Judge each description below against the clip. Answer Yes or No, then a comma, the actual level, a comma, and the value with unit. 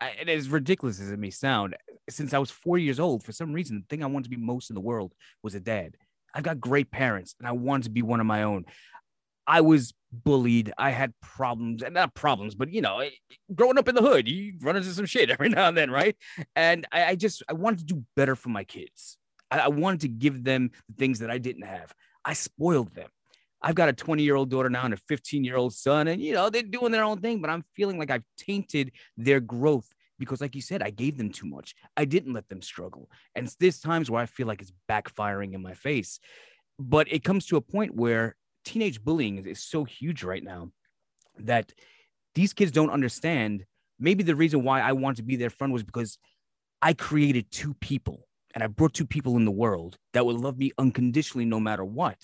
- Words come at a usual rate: No, fast, 230 wpm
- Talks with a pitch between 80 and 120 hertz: No, low, 135 Hz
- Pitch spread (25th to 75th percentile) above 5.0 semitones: Yes, wide, 5.6 semitones